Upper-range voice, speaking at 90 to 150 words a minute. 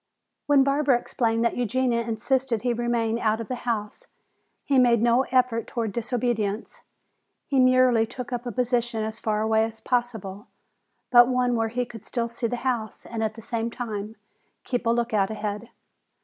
No: high, 235 Hz; average, 175 wpm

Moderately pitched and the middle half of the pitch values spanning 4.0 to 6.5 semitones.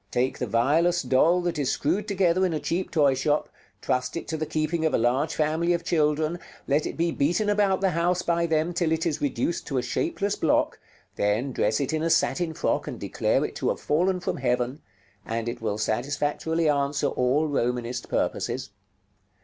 Yes: medium, 155 Hz; average, 4.7 semitones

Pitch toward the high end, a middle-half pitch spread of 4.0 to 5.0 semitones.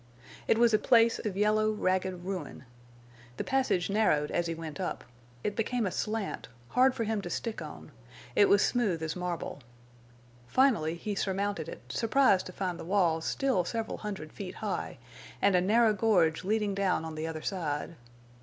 Yes: high, 195 Hz; average, 4.5 semitones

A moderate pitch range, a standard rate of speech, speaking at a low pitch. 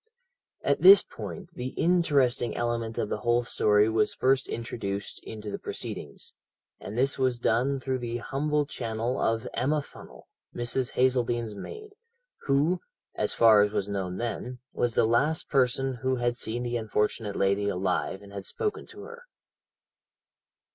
Yes: average, 3.7 semitones; average, 155 wpm; low, 120 Hz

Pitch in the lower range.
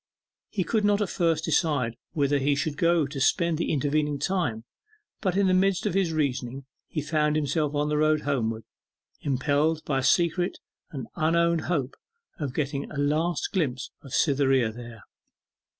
No: medium, 150 Hz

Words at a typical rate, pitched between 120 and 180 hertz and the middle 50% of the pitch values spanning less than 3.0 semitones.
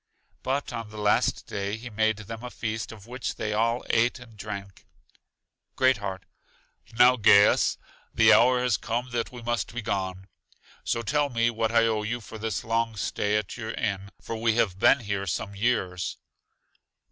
No: average, 180 wpm; low, 110 Hz; narrow, 2.5 semitones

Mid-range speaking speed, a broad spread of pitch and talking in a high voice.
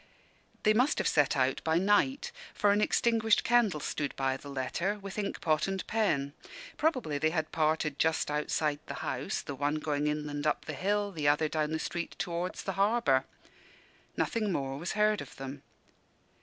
No: average, 180 wpm; wide, 5.9 semitones; medium, 160 Hz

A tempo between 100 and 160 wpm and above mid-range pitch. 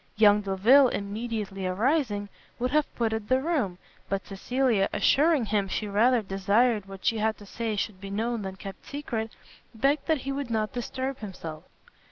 No: average, 170 wpm; high, 220 Hz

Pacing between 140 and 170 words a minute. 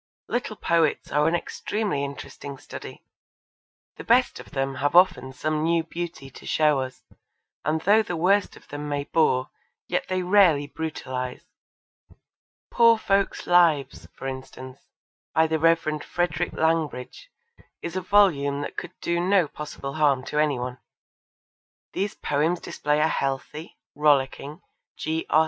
Yes: average, 145 wpm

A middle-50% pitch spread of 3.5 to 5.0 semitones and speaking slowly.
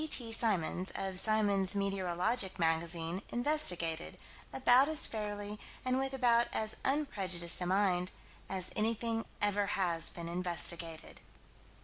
Yes: average, 4.5 semitones; slow, 115 wpm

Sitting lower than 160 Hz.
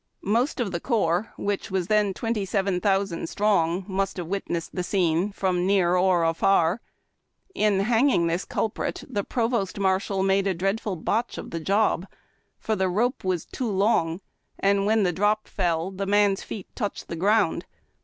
No: high, 195 Hz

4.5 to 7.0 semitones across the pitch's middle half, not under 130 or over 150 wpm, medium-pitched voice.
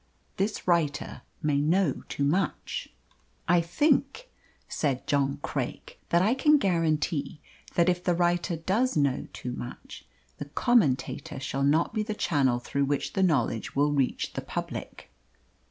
Yes: average, 5.2 semitones; average, 145 wpm; medium, 165 Hz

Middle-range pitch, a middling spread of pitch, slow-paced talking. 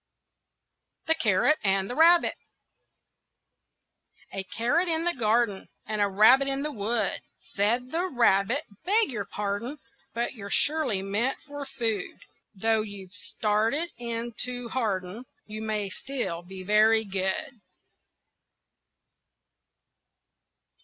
No: high, 225 Hz; average, 4.9 semitones; slow, 115 wpm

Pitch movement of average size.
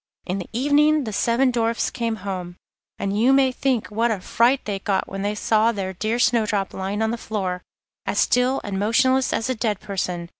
Yes: average, 3.8 semitones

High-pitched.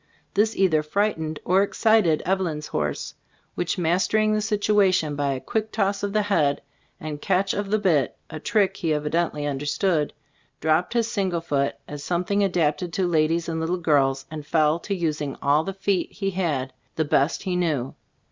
No: medium, 170 Hz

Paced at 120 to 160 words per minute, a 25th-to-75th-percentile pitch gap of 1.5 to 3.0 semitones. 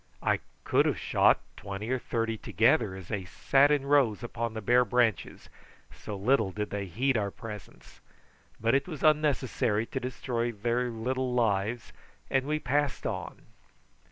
No: average, 155 wpm; average, 3.7 semitones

